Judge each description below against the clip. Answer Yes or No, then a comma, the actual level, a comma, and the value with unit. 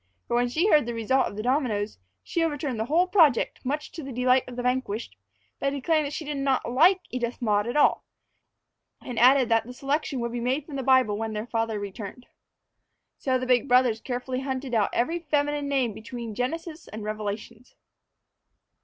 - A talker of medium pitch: No, very high, 255 Hz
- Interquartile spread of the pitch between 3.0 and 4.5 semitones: Yes, average, 3.6 semitones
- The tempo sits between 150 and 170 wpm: No, average, 195 wpm